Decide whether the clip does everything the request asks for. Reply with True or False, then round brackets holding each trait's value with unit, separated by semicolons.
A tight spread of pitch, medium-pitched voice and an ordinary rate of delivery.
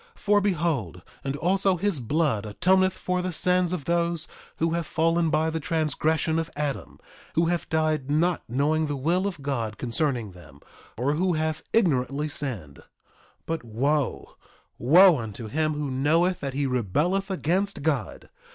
False (4.2 semitones; 155 Hz; 160 wpm)